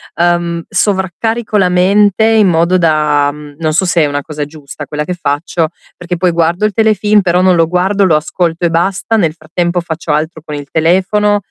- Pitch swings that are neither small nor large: Yes, average, 3.4 semitones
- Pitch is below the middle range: No, medium, 175 Hz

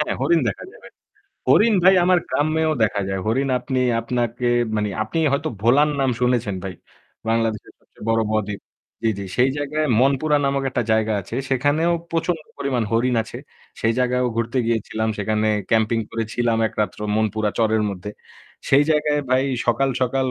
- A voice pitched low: Yes, low, 120 Hz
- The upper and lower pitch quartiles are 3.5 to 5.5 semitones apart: Yes, average, 4.2 semitones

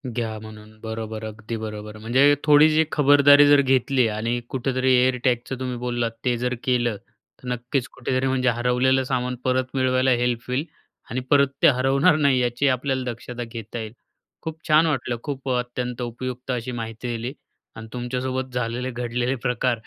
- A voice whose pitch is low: Yes, low, 125 Hz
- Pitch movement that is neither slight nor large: No, narrow, 1.8 semitones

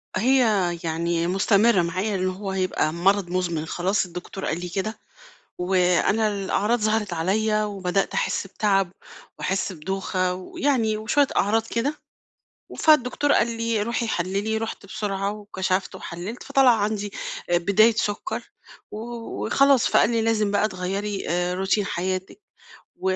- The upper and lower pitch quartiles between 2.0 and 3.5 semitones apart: Yes, average, 3.1 semitones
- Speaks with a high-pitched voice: Yes, high, 200 Hz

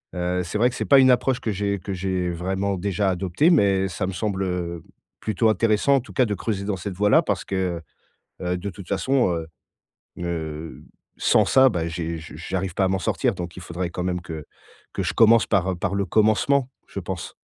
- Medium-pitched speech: No, very low, 95 Hz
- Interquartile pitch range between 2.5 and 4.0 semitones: Yes, average, 3.2 semitones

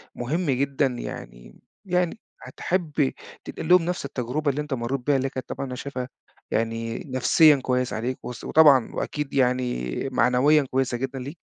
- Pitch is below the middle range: Yes, low, 130 Hz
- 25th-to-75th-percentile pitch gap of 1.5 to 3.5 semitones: Yes, average, 3.1 semitones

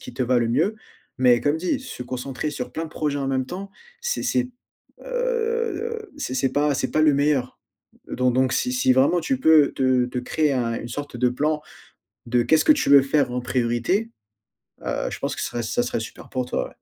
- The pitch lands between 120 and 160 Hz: Yes, medium, 140 Hz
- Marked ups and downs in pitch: Yes, wide, 6.5 semitones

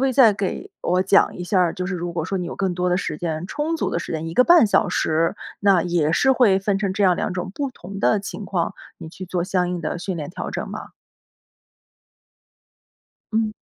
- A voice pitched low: No, medium, 185 Hz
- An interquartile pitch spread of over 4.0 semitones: No, average, 2.7 semitones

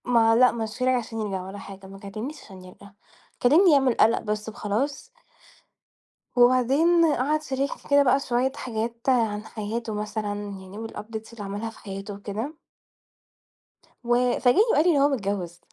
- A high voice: Yes, high, 225 Hz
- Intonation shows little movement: No, average, 3.8 semitones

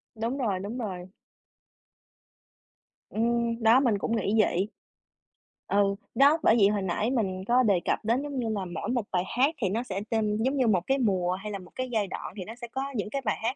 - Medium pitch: No, high, 220 Hz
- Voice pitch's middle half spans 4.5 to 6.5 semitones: No, average, 3.8 semitones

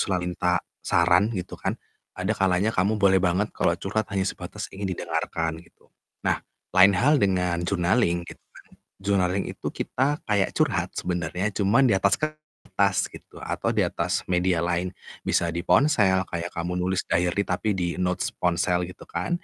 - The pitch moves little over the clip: Yes, narrow, 2.2 semitones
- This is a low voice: Yes, very low, 95 Hz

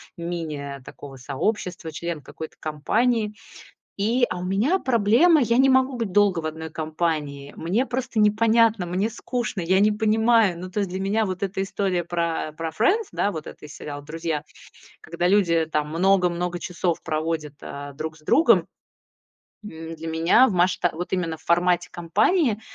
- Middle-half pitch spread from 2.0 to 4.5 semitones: No, average, 4.9 semitones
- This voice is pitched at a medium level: Yes, medium, 180 Hz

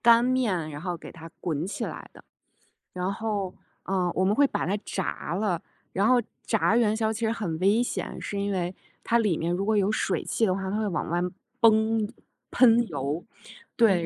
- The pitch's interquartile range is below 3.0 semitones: No, average, 3.9 semitones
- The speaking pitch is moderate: No, high, 200 Hz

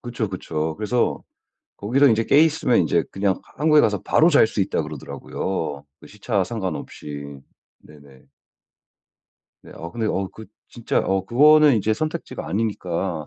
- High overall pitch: No, low, 100 Hz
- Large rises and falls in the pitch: Yes, wide, 6.2 semitones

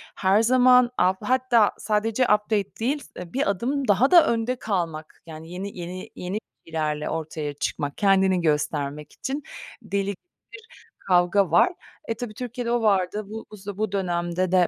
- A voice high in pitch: Yes, high, 195 Hz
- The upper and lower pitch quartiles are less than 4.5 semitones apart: No, average, 5.1 semitones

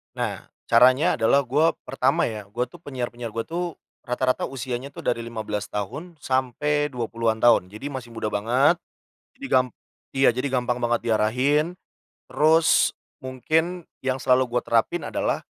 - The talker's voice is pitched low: Yes, low, 125 Hz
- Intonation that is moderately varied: Yes, average, 3.5 semitones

